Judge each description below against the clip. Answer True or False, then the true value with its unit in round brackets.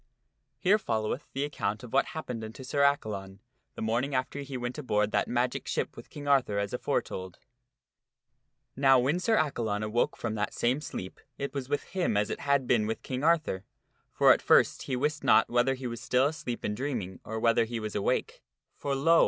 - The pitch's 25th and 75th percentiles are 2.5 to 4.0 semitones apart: False (4.4 semitones)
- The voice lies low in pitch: True (125 Hz)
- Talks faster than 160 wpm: True (200 wpm)